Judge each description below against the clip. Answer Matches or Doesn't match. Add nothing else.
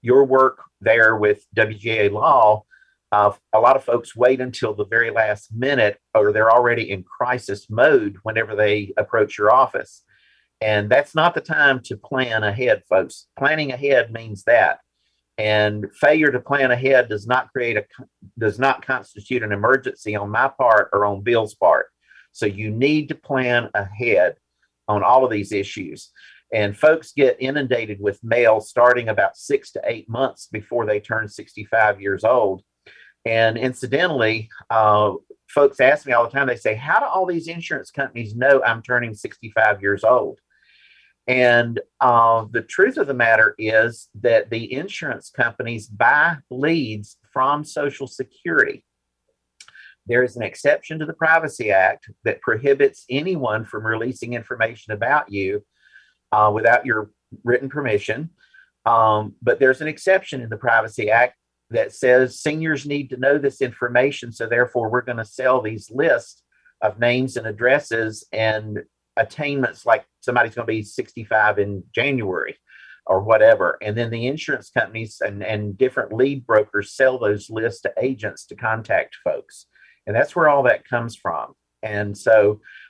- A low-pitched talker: Matches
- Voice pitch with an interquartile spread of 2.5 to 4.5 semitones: Matches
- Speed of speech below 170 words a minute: Matches